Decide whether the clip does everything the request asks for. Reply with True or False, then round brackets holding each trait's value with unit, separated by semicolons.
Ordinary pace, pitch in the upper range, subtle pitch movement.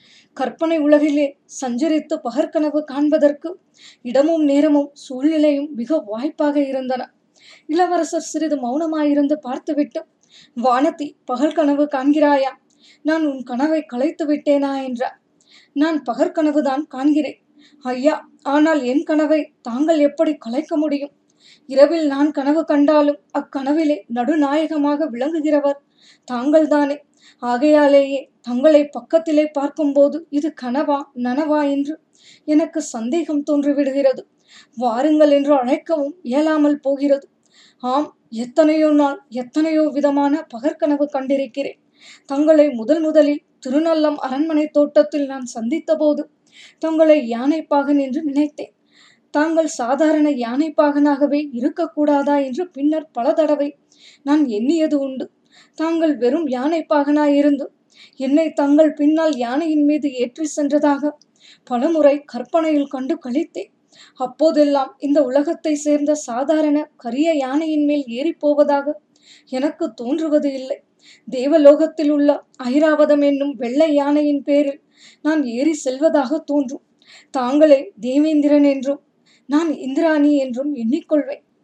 True (100 wpm; 295 Hz; 1.8 semitones)